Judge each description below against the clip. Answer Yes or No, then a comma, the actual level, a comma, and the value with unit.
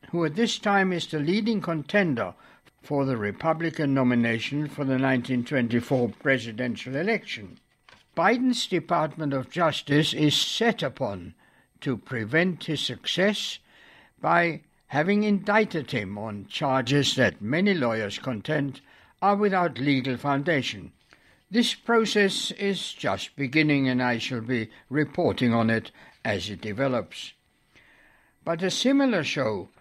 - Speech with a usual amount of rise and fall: No, wide, 6.4 semitones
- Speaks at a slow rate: Yes, slow, 125 wpm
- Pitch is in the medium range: Yes, medium, 150 Hz